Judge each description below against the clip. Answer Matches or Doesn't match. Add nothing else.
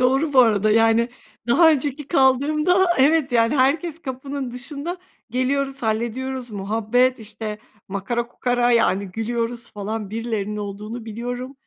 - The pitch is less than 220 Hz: Doesn't match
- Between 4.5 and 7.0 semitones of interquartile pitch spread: Doesn't match